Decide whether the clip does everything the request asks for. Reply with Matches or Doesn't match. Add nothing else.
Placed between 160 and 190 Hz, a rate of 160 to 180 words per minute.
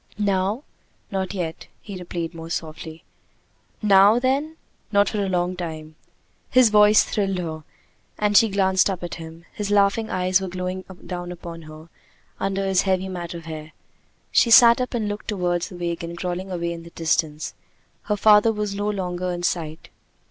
Matches